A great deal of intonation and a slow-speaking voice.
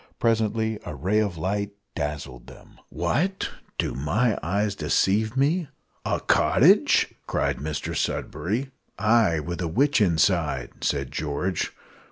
Yes: wide, 6.6 semitones; slow, 125 wpm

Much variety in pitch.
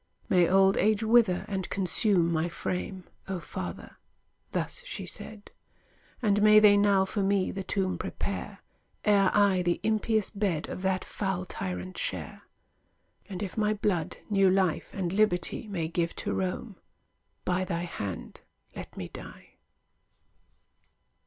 No: narrow, 2.6 semitones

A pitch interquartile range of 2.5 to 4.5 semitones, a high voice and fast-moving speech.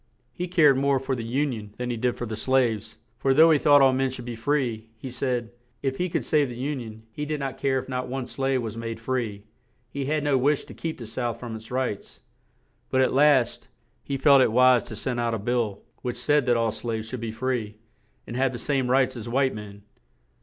No: average, 2.8 semitones; low, 125 Hz; fast, 240 wpm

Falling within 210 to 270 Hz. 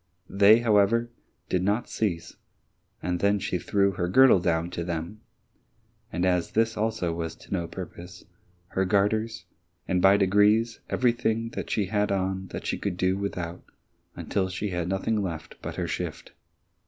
No: very low, 95 Hz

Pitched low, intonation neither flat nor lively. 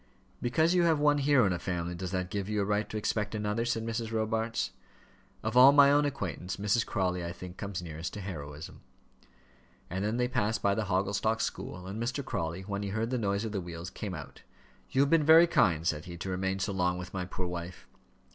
Yes: low, 100 Hz; average, 4.2 semitones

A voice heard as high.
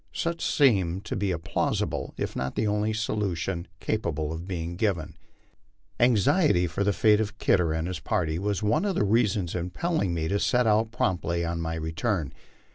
No: very low, 95 Hz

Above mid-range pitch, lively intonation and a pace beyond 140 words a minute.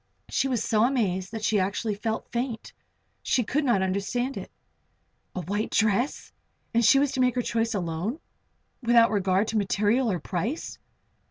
No: high, 220 Hz; average, 3.5 semitones; average, 160 wpm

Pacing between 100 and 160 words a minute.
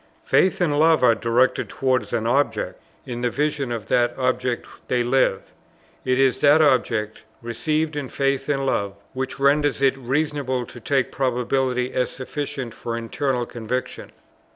Yes: average, 155 wpm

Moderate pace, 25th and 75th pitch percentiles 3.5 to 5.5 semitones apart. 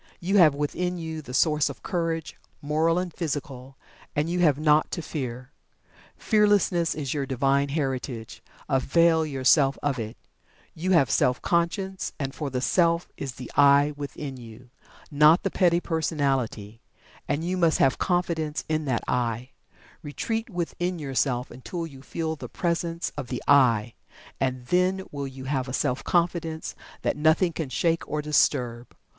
Yes: average, 155 wpm; average, 4.2 semitones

